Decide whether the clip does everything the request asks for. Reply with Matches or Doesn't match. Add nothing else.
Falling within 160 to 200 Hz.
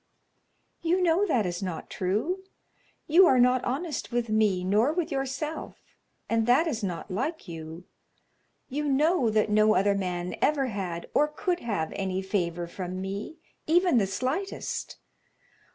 Doesn't match